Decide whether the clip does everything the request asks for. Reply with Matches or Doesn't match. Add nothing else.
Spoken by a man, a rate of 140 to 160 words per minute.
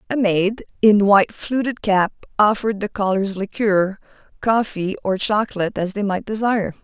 Doesn't match